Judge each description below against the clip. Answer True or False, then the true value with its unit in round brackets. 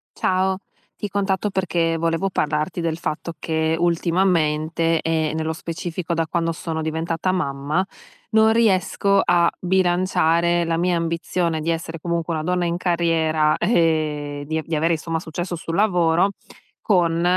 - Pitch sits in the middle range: True (170 Hz)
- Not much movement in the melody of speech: True (2.0 semitones)